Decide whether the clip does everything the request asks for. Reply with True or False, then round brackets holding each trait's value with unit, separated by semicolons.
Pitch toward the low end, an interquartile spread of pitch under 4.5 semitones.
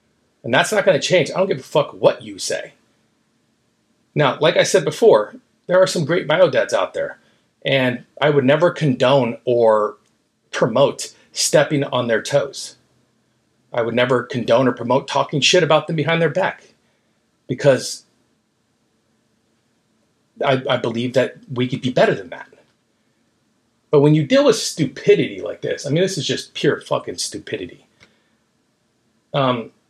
False (130 Hz; 5.4 semitones)